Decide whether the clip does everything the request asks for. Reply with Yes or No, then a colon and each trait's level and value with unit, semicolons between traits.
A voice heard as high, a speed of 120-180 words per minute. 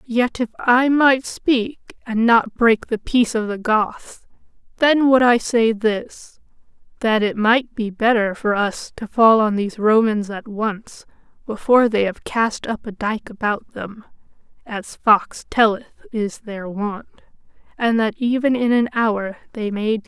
Yes: high, 220 Hz; average, 170 wpm